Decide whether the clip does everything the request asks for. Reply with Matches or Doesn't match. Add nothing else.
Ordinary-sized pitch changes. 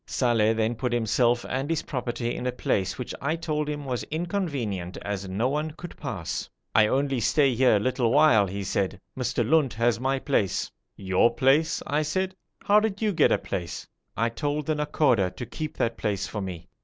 Doesn't match